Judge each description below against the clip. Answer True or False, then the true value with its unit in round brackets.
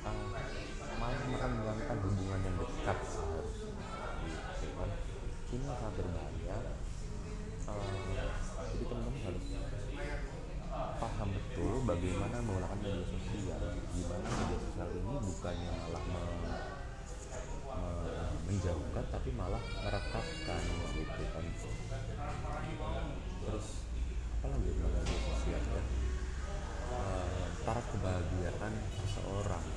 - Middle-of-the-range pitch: False (95 Hz)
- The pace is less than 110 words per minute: True (85 wpm)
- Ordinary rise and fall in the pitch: True (3.6 semitones)